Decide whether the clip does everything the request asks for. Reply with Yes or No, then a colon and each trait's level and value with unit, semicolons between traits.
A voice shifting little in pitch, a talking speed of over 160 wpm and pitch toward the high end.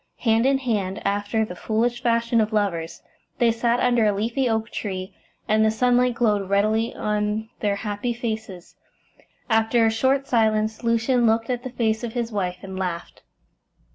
Yes: narrow, 2.3 semitones; average, 170 wpm; high, 220 Hz